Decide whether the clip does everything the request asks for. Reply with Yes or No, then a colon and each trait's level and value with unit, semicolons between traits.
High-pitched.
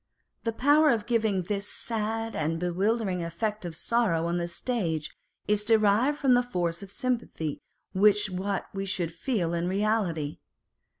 Yes: high, 200 Hz